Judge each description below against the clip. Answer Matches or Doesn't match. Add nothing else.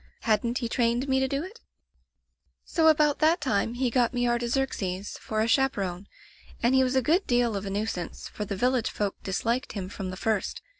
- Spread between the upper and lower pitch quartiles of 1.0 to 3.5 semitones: Doesn't match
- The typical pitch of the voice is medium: Doesn't match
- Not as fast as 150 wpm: Doesn't match